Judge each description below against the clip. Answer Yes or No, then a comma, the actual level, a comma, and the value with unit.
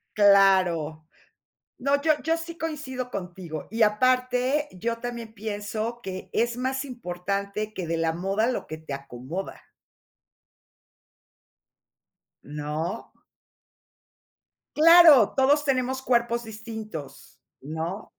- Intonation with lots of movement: Yes, wide, 6.1 semitones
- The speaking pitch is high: Yes, high, 220 Hz